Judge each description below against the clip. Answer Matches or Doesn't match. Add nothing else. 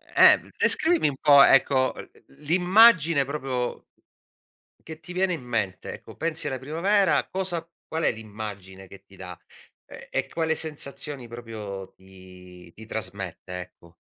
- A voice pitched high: Doesn't match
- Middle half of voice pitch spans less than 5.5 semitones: Doesn't match